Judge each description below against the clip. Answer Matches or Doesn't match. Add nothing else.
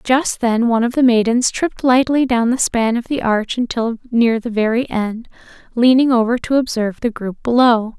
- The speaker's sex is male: Doesn't match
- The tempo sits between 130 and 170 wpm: Doesn't match